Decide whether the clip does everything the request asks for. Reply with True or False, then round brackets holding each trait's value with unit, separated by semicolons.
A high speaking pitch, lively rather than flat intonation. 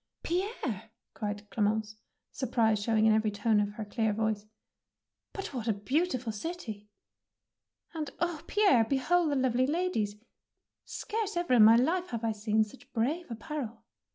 True (230 Hz; 6.5 semitones)